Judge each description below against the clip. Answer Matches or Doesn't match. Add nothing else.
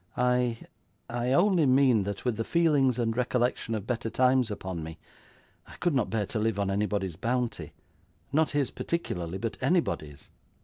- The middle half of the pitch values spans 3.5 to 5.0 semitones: Matches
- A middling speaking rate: Matches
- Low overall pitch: Matches